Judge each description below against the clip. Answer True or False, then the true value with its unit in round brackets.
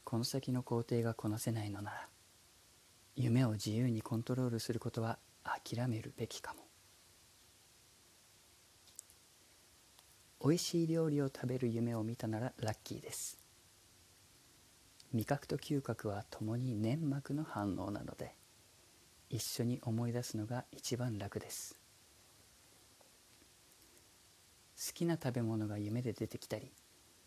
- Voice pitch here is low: True (115 Hz)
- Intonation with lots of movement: False (2.7 semitones)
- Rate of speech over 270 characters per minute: False (230 characters per minute)